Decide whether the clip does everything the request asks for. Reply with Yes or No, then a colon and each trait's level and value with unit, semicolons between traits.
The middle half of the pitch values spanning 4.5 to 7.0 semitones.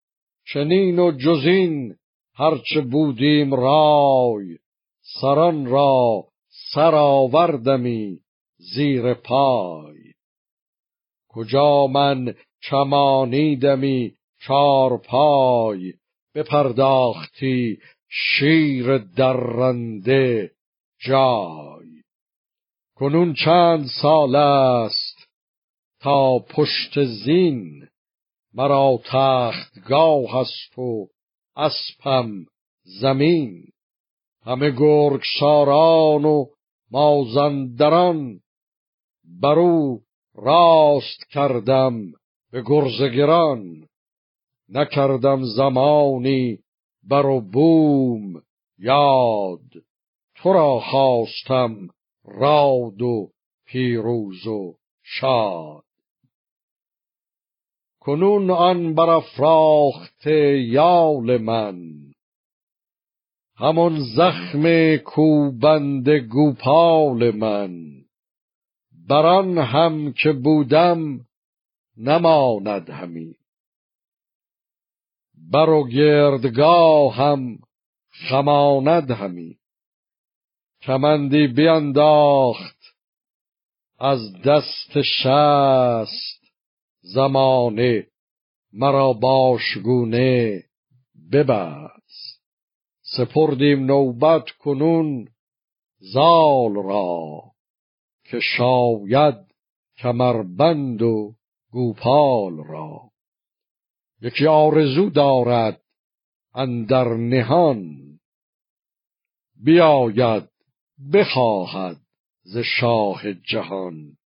No: average, 3.9 semitones